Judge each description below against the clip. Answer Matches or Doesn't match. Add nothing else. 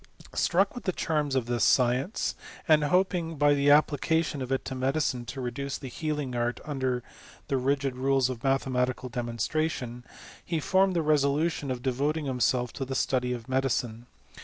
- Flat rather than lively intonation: Doesn't match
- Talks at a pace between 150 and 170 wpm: Matches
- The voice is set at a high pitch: Doesn't match